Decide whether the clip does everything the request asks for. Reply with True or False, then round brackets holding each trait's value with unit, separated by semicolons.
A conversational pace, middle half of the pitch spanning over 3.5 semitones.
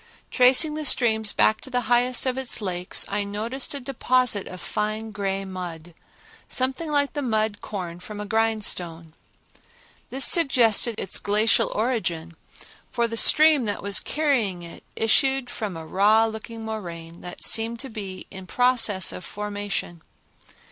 True (155 wpm; 4.3 semitones)